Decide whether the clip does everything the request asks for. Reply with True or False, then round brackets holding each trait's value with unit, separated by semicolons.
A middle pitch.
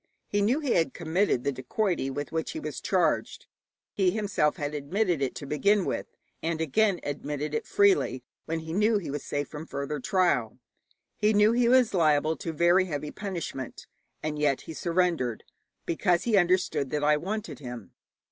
True (165 Hz)